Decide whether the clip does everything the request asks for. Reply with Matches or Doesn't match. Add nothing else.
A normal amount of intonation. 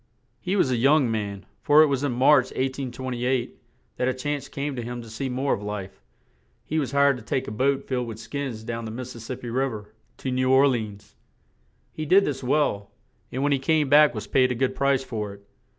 Matches